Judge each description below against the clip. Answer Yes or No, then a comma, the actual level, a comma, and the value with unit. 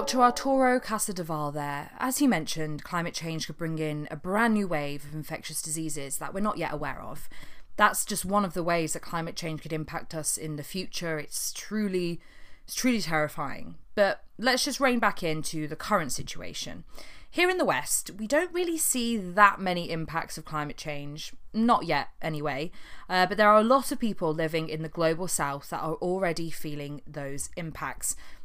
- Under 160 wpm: No, average, 190 wpm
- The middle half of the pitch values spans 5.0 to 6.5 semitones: Yes, average, 5.3 semitones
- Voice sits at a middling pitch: Yes, medium, 165 Hz